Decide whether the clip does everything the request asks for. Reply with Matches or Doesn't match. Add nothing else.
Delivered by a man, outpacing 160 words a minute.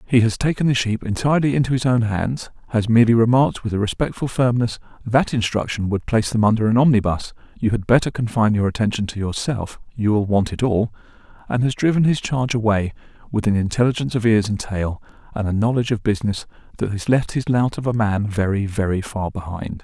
Matches